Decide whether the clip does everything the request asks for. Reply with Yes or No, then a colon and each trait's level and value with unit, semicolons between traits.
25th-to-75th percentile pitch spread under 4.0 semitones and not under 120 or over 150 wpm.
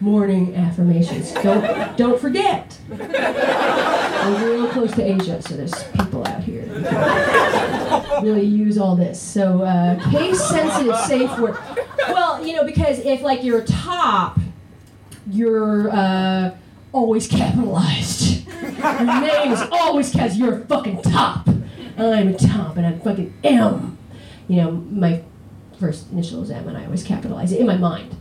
No: average, 5.1 semitones; average, 145 wpm